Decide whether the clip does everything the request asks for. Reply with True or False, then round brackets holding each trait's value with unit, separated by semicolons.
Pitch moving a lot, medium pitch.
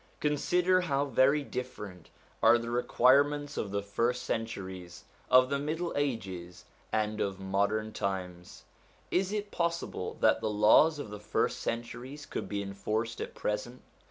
False (6.1 semitones; 115 Hz)